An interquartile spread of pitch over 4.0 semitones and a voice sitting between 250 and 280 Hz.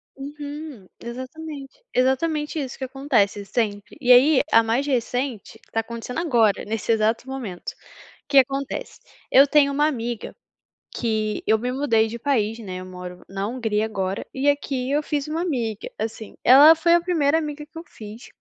Yes: average, 4.7 semitones; very high, 255 Hz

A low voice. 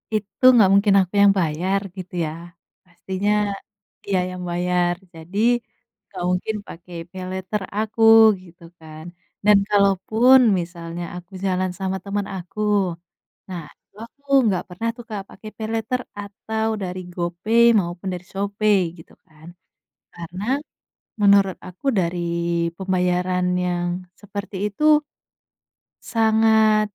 No: high, 190 Hz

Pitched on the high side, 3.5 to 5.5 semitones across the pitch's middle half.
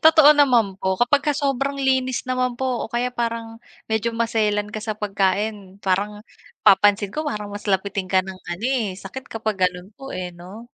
Yes: high, 220 Hz; average, 4.2 semitones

